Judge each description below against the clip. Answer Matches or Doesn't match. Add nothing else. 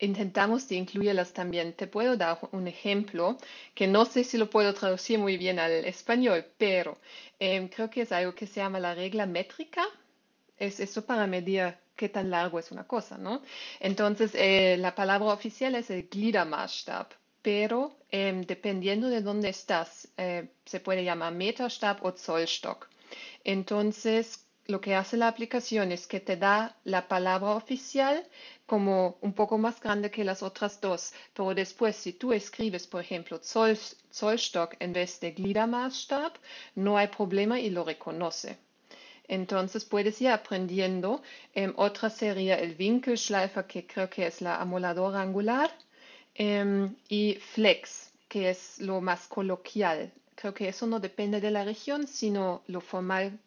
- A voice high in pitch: Matches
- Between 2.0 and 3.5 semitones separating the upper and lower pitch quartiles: Matches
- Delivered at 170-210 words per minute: Doesn't match